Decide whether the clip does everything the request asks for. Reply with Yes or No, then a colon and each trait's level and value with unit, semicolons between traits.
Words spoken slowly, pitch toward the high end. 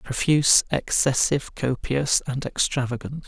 No: slow, 90 wpm; low, 135 Hz